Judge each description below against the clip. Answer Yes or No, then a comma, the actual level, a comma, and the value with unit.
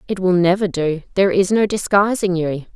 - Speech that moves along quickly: No, average, 195 wpm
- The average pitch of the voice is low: No, medium, 185 Hz